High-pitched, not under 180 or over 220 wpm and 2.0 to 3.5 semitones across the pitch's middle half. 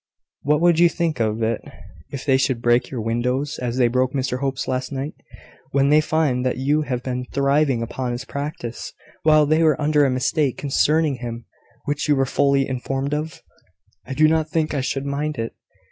No: low, 135 Hz; average, 195 wpm; average, 3.0 semitones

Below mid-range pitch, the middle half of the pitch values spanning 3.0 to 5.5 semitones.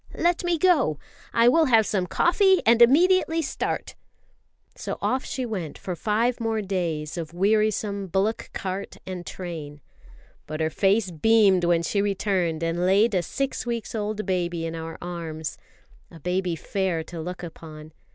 No: high, 190 Hz; average, 5.0 semitones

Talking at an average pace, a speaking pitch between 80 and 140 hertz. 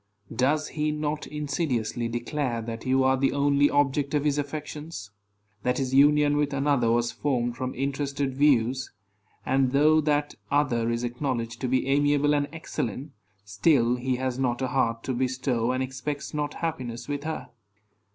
Yes: average, 160 wpm; low, 135 Hz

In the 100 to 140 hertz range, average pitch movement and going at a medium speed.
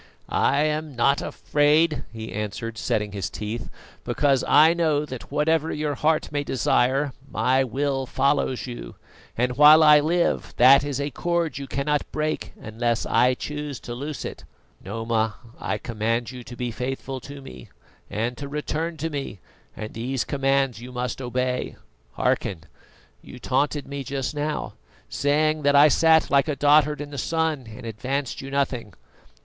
Yes: low, 135 Hz; average, 3.4 semitones; average, 160 wpm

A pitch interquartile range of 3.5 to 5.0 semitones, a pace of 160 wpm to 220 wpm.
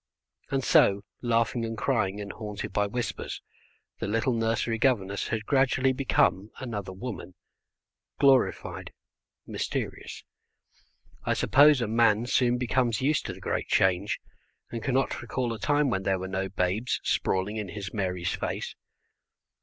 No: average, 4.3 semitones; average, 140 wpm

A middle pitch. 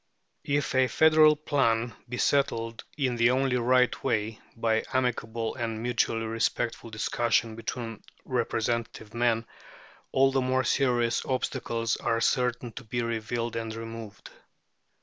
No: low, 120 Hz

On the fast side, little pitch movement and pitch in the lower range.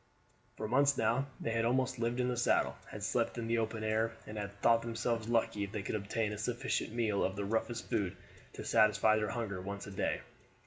Yes: fast, 220 wpm; narrow, 2.0 semitones; low, 115 Hz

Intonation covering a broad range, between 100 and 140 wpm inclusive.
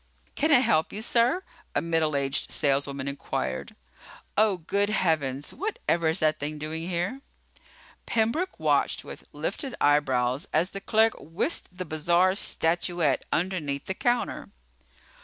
Yes: wide, 6.5 semitones; slow, 135 wpm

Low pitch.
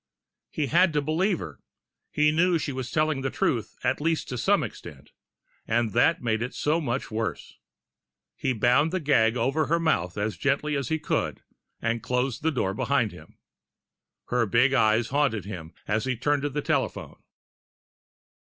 Yes: low, 130 Hz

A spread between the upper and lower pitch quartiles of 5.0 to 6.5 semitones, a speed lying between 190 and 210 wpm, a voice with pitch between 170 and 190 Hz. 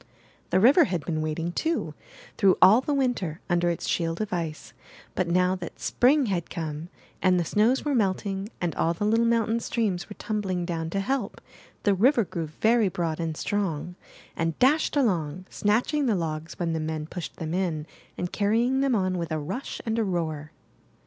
Yes: average, 5.3 semitones; average, 200 wpm; medium, 185 Hz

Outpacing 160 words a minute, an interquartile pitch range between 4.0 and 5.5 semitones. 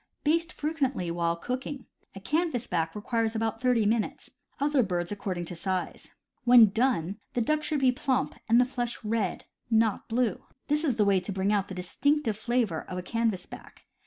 Yes: average, 185 wpm; average, 5.1 semitones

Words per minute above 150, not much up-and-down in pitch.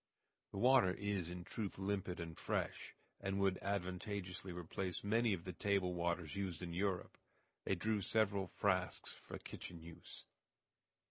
No: average, 145 wpm; narrow, 2.3 semitones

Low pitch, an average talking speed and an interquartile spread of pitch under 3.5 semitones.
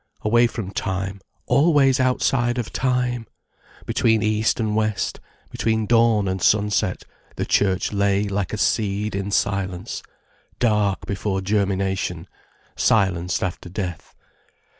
No: low, 105 Hz; slow, 120 wpm; average, 2.9 semitones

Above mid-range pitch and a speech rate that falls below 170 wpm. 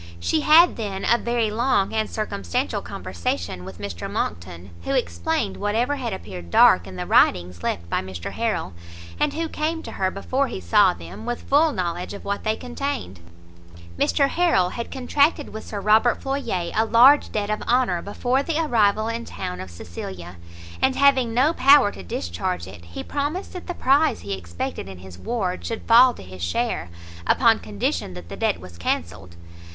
No: high, 200 Hz; average, 180 wpm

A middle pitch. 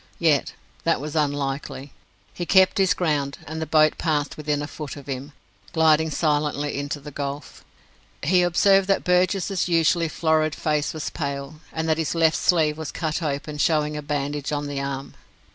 Yes: medium, 155 Hz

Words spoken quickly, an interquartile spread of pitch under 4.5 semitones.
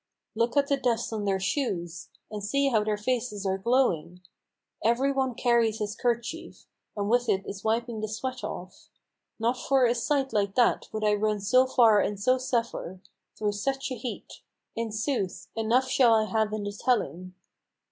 No: average, 180 wpm; average, 3.6 semitones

